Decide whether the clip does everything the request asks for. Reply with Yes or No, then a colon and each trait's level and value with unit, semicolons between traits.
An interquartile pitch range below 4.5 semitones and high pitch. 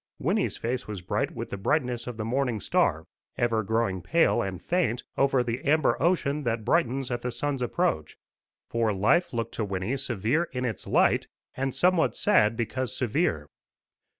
No: average, 4.1 semitones; low, 120 Hz